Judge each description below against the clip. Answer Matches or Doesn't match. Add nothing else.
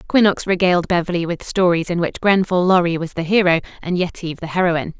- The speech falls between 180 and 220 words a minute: Matches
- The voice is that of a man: Doesn't match